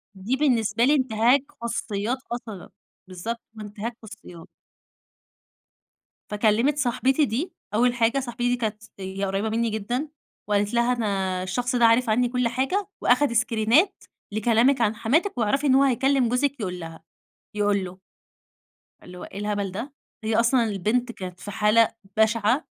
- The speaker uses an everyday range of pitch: Yes, average, 3.2 semitones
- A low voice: No, high, 230 Hz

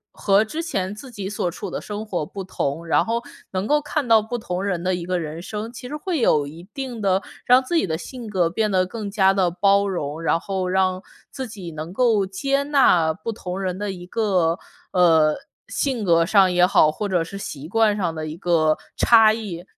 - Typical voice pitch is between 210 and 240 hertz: No, high, 190 Hz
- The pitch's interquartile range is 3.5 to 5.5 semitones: Yes, average, 4.2 semitones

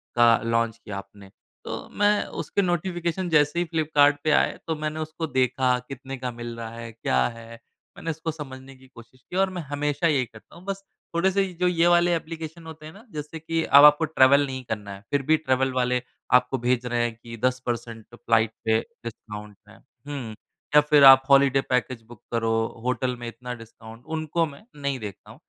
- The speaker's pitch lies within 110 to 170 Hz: Yes, low, 135 Hz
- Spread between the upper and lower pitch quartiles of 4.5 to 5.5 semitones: Yes, average, 5.2 semitones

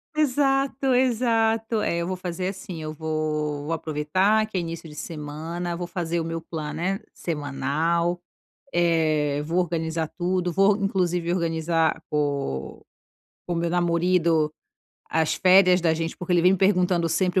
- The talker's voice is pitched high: No, medium, 170 Hz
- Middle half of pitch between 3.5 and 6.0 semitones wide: No, narrow, 2.6 semitones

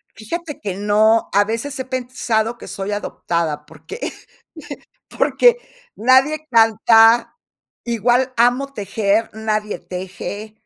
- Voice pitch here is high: Yes, high, 225 Hz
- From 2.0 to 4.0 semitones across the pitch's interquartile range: Yes, average, 3.6 semitones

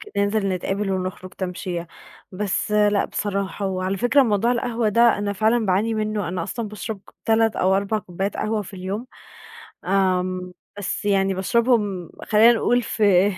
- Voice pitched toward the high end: Yes, high, 200 Hz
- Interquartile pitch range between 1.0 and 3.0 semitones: Yes, average, 2.7 semitones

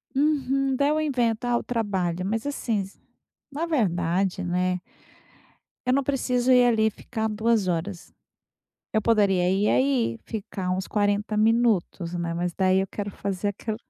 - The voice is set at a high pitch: Yes, high, 210 Hz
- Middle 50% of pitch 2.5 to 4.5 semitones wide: No, average, 4.9 semitones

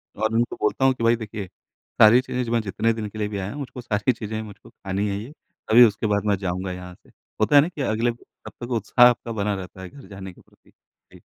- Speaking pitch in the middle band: No, low, 110 Hz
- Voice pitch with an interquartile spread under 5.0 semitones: Yes, average, 2.9 semitones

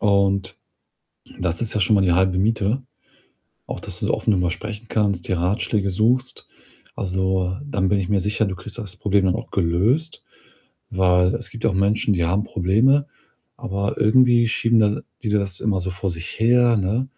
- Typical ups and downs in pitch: Yes, average, 3.1 semitones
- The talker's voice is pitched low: Yes, low, 100 Hz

